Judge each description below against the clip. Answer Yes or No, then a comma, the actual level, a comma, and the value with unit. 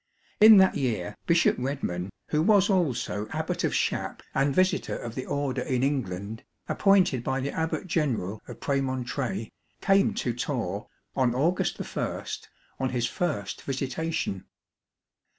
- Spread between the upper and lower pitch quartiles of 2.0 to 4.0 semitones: No, wide, 5.6 semitones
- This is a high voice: No, low, 135 Hz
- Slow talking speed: No, average, 145 wpm